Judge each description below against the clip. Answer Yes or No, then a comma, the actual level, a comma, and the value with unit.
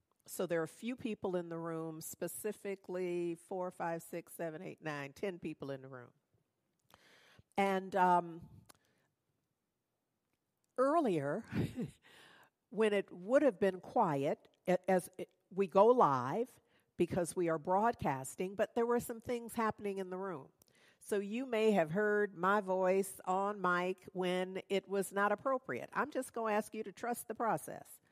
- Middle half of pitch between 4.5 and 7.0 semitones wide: No, average, 3.7 semitones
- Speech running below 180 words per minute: Yes, average, 155 wpm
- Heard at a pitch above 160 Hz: Yes, high, 190 Hz